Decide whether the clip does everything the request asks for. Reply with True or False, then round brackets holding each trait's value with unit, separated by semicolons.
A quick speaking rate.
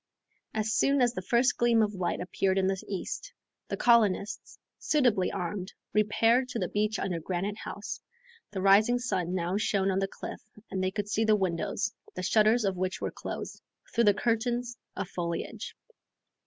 False (175 wpm)